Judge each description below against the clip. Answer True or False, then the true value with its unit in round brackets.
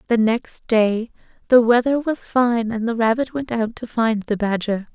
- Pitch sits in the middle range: False (230 Hz)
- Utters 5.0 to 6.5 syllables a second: False (4.4 syllables/s)